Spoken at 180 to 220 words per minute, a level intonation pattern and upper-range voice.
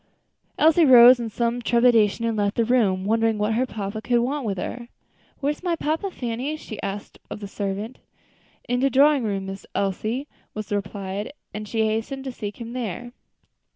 No: average, 185 wpm; average, 3.5 semitones; high, 230 Hz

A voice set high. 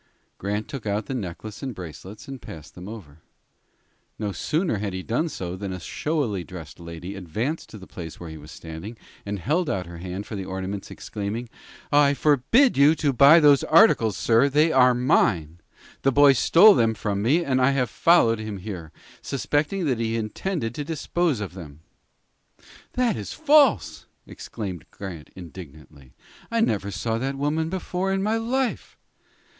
No: low, 115 Hz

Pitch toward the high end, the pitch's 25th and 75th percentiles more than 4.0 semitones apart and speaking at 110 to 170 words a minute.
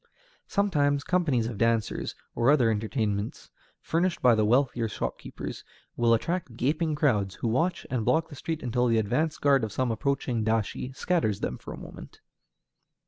No: low, 125 Hz; average, 5.1 semitones; average, 160 wpm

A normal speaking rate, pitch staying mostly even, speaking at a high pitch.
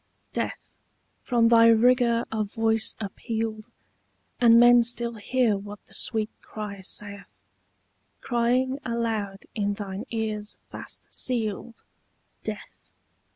No: slow, 110 wpm; narrow, 2.2 semitones; high, 225 Hz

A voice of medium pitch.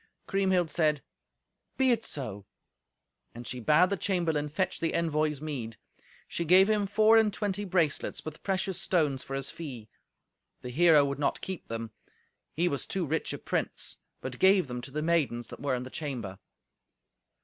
Yes: medium, 155 Hz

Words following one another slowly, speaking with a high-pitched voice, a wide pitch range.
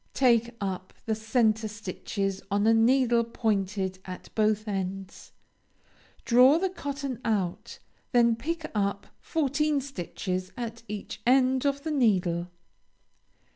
No: slow, 120 wpm; high, 225 Hz; average, 4.6 semitones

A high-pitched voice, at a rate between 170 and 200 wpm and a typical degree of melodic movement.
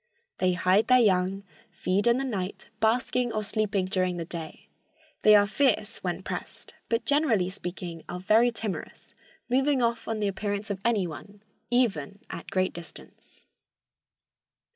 No: high, 205 Hz; average, 150 wpm; average, 4.1 semitones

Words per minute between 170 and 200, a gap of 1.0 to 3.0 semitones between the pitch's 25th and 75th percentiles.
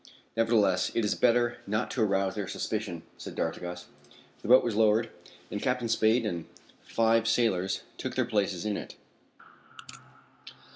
No: average, 145 wpm; average, 2.7 semitones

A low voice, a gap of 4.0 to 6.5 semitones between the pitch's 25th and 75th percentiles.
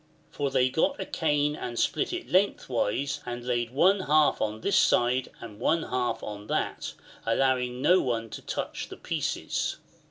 Yes: low, 130 Hz; average, 4.4 semitones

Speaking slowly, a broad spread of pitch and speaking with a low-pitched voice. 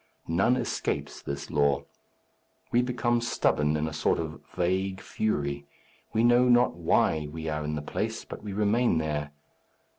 No: average, 155 wpm; wide, 7.9 semitones; very low, 85 Hz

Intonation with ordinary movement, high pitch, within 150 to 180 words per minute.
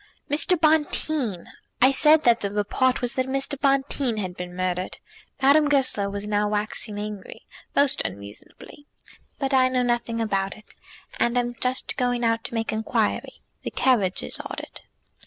Yes: average, 4.6 semitones; high, 240 Hz; average, 155 wpm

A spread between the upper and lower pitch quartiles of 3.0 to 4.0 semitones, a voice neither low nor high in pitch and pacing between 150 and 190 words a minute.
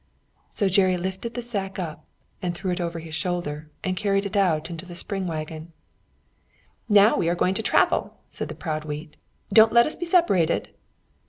Yes: average, 3.3 semitones; medium, 180 Hz; average, 185 wpm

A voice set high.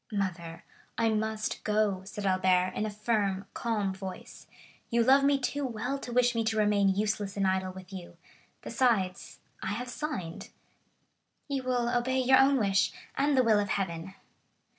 Yes: high, 215 Hz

